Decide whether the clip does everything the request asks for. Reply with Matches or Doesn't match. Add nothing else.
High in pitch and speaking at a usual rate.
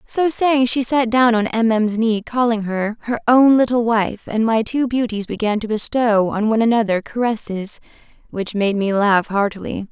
Matches